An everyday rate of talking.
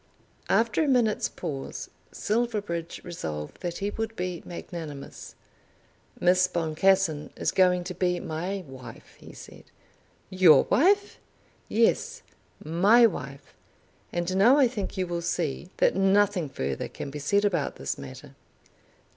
No: slow, 130 wpm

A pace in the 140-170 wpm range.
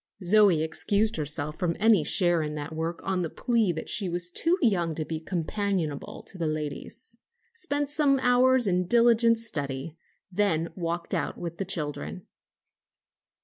Yes: average, 155 wpm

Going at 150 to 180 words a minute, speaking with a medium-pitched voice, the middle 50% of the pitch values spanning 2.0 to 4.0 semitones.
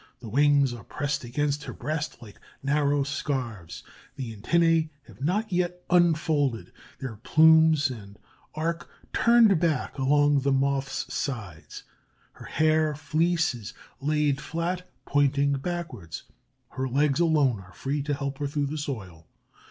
No: slow, 135 wpm; medium, 145 Hz; average, 3.2 semitones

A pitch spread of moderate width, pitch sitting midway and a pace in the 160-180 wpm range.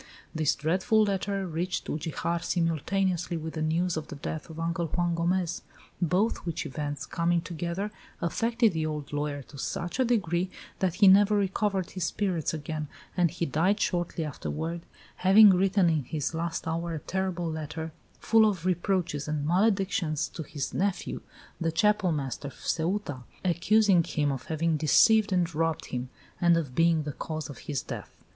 Yes: average, 3.3 semitones; medium, 170 Hz; average, 165 wpm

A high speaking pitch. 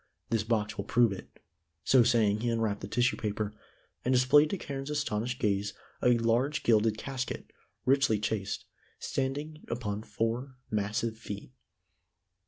No: low, 115 Hz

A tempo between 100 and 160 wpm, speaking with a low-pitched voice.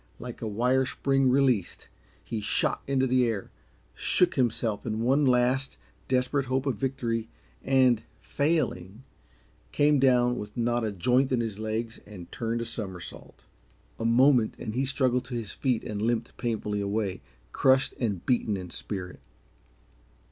Yes: average, 150 wpm; low, 120 Hz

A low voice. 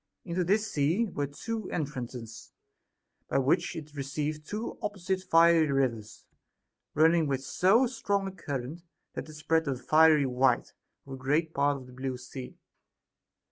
No: medium, 150 Hz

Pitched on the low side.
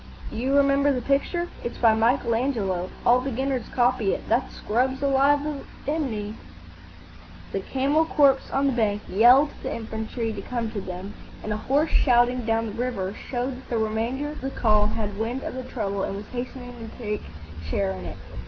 No: high, 240 Hz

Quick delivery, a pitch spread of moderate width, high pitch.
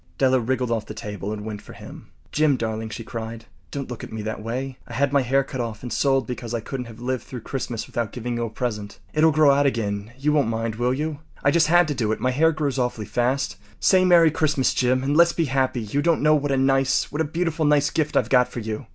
No: fast, 255 wpm; average, 4.0 semitones; low, 130 Hz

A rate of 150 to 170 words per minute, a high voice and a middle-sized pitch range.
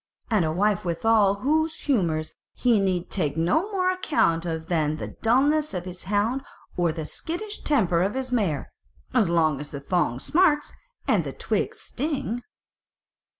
No: average, 165 wpm; high, 200 Hz; wide, 8.5 semitones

